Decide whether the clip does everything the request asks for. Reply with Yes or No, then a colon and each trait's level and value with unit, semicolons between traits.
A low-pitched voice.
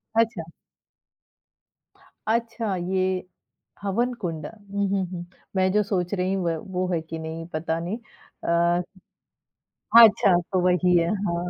No: medium, 185 Hz